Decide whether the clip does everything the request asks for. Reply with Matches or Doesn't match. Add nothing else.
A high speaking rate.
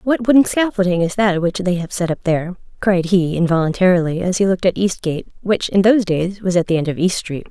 Matches